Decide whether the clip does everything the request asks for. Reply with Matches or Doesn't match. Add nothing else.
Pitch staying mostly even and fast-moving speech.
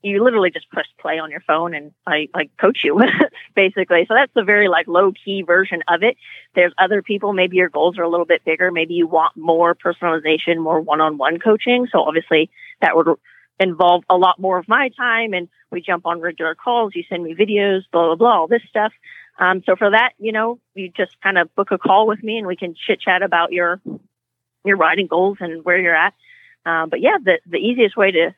Doesn't match